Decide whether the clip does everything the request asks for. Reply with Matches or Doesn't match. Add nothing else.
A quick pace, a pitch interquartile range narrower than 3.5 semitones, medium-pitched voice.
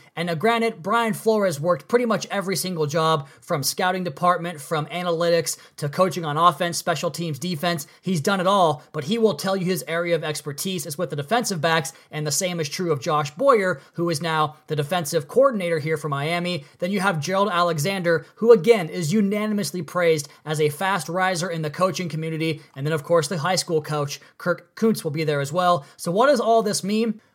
Matches